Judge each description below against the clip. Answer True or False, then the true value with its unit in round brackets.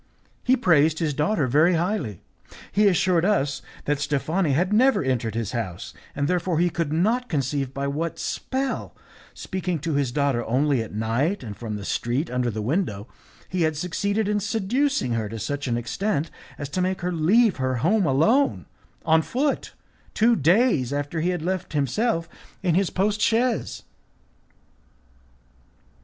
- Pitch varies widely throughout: True (6.5 semitones)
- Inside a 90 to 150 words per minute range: False (160 wpm)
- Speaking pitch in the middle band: True (160 Hz)